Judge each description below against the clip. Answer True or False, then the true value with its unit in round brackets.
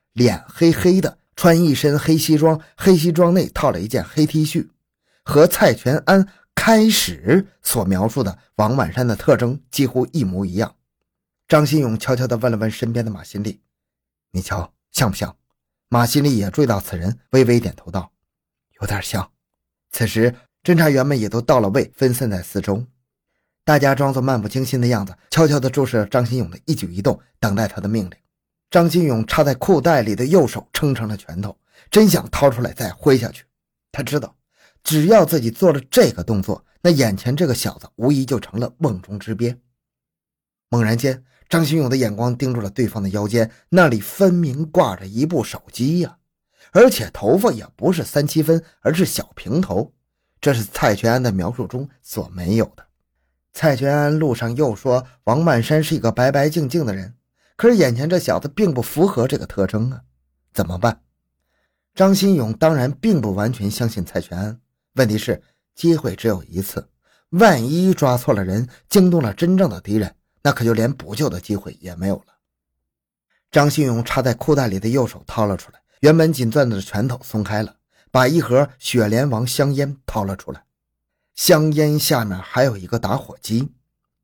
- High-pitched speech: False (125 Hz)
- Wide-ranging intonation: True (6.5 semitones)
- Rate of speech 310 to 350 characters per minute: False (265 characters per minute)